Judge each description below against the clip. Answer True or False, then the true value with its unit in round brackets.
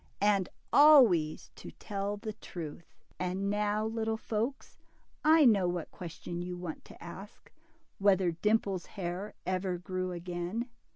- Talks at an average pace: False (130 wpm)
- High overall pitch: True (195 Hz)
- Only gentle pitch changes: False (3.3 semitones)